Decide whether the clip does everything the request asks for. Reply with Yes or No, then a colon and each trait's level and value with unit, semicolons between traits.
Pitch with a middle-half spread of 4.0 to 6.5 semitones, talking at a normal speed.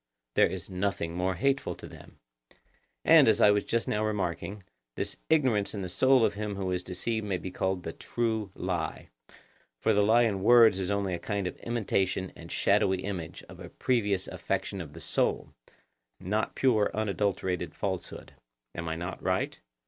No: average, 2.9 semitones; average, 180 wpm